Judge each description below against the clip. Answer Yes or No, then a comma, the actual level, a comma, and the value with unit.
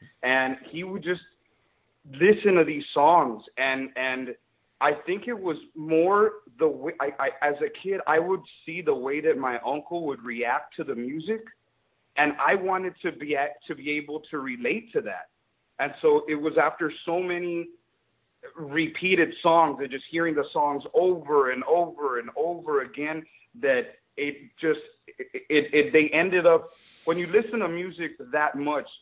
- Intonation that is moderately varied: Yes, average, 4.2 semitones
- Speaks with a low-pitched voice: No, medium, 165 Hz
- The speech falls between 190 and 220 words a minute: No, average, 175 wpm